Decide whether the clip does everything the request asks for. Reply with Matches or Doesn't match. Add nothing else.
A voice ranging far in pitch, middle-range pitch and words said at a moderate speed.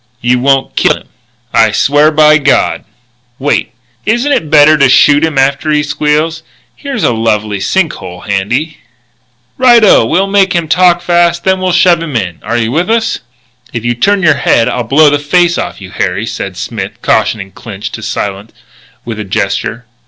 Matches